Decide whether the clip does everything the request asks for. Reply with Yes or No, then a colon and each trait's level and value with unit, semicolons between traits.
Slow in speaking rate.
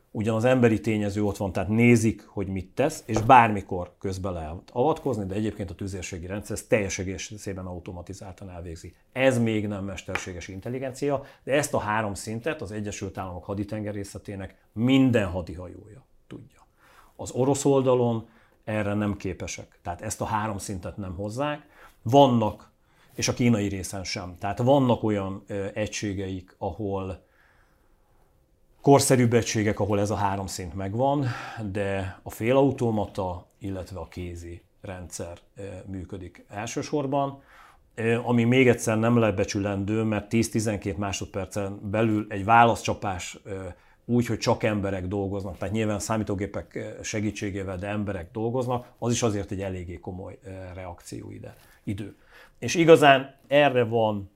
No: average, 130 wpm